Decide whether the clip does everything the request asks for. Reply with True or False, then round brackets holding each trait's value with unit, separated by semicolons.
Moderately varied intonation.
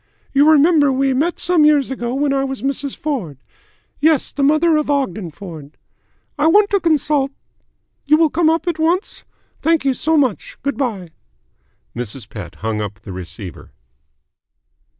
False (8.5 semitones)